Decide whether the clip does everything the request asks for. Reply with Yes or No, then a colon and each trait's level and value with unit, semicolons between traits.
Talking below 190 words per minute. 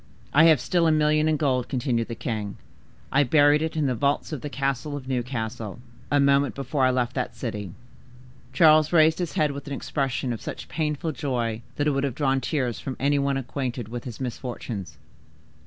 No: average, 200 wpm